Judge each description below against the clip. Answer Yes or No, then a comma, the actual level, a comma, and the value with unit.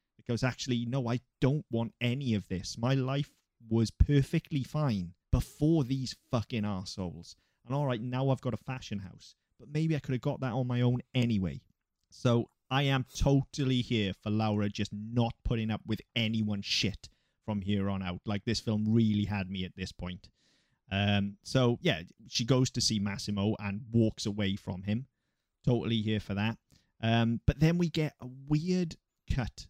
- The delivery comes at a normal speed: Yes, average, 185 wpm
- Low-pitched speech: Yes, low, 115 Hz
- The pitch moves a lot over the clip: No, average, 4.1 semitones